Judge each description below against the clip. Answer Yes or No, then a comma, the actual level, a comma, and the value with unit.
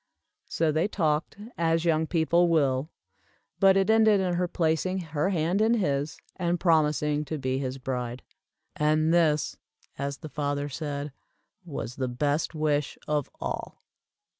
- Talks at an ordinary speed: Yes, average, 145 wpm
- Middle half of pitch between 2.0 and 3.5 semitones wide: Yes, average, 3.1 semitones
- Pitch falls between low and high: Yes, medium, 155 Hz